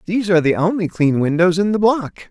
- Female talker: No, male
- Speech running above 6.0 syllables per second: Yes, 6.3 syllables/s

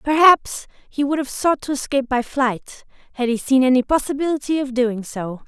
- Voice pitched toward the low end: No, very high, 265 Hz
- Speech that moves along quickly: No, average, 185 wpm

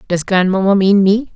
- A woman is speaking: No, male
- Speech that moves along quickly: No, average, 180 wpm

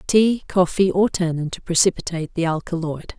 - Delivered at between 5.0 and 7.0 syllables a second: Yes, 5.3 syllables/s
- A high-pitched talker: No, medium, 175 Hz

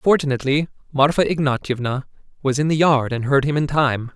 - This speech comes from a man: Yes, male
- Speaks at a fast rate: No, average, 175 wpm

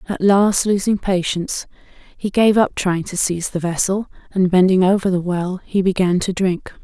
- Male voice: No, female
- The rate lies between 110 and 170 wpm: No, average, 185 wpm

